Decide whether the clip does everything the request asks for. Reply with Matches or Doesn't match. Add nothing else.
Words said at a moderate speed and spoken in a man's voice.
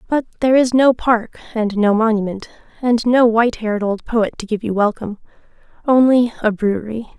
Doesn't match